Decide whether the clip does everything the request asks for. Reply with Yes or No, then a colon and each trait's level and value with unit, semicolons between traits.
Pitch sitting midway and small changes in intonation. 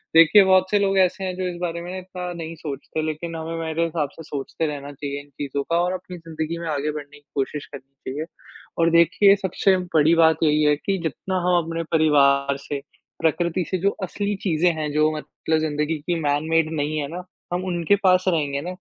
No: medium, 160 Hz; average, 3.2 semitones